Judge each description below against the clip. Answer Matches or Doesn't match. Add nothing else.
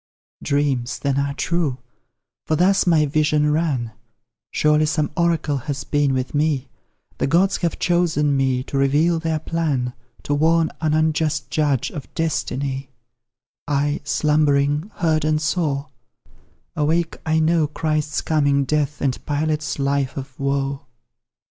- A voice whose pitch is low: Doesn't match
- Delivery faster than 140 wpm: Doesn't match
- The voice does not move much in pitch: Matches